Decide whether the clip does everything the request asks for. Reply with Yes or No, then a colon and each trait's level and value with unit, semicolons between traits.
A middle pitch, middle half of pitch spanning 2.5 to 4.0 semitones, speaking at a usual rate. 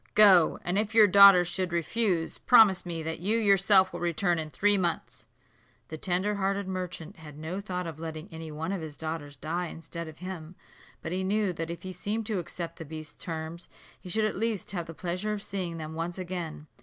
No: medium, 175 Hz; average, 3.4 semitones; fast, 210 wpm